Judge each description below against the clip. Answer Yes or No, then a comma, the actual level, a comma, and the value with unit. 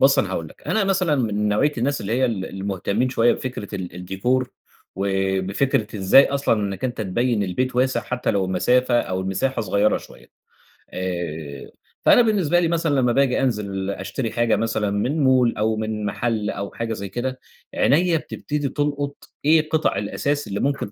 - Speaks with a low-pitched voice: Yes, low, 115 Hz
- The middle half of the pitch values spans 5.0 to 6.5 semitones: Yes, average, 5.3 semitones